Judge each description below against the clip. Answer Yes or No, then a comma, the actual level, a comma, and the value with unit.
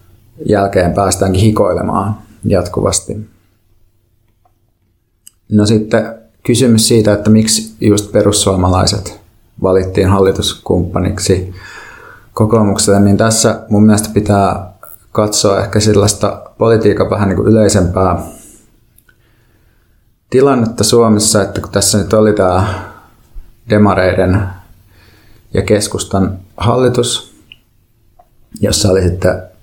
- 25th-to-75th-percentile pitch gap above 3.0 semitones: No, narrow, 2.4 semitones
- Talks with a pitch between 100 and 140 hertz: Yes, low, 105 Hz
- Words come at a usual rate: No, slow, 90 wpm